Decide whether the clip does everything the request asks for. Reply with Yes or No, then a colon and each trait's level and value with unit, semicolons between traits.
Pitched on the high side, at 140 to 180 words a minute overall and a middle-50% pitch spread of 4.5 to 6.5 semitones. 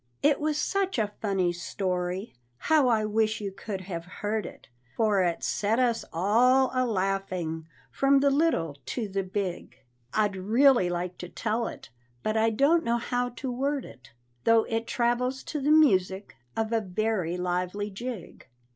Yes: high, 215 Hz; average, 165 wpm; average, 5.1 semitones